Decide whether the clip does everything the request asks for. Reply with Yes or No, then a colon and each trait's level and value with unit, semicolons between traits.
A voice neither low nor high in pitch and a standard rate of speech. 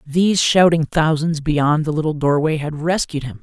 Yes: medium, 155 Hz; average, 175 wpm